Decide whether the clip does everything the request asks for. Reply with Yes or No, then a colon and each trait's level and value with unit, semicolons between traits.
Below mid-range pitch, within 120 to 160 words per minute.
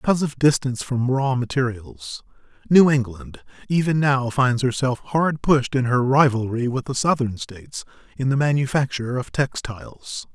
Yes: low, 130 Hz; average, 150 wpm